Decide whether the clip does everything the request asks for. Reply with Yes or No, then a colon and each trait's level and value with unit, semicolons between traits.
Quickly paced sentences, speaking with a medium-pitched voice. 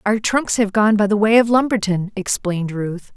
No: fast, 210 wpm; high, 205 Hz